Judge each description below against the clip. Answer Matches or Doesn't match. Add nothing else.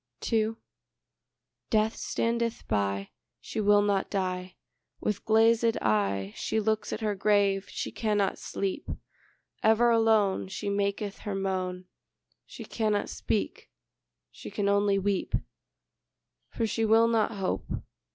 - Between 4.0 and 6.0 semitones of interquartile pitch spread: Doesn't match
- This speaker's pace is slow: Matches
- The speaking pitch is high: Matches